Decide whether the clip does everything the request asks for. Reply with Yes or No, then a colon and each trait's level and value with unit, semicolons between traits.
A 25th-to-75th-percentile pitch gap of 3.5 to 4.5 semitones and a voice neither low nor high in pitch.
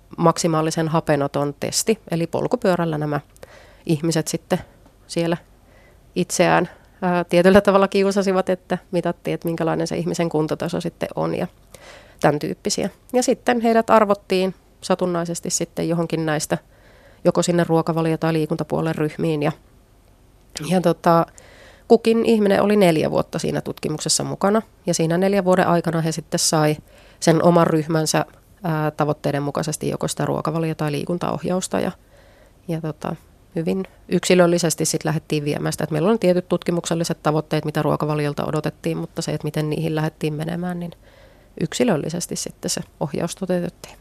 No: average, 2.8 semitones; medium, 165 Hz